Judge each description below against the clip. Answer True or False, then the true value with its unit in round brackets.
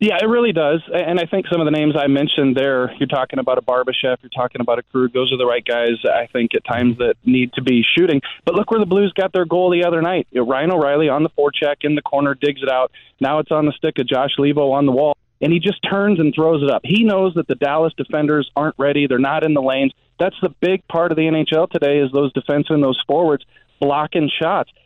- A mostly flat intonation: False (3.8 semitones)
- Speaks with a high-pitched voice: False (145 Hz)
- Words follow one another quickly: True (255 wpm)